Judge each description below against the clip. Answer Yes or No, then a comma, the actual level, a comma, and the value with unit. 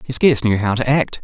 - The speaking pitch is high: No, low, 120 Hz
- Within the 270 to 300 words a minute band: Yes, fast, 290 wpm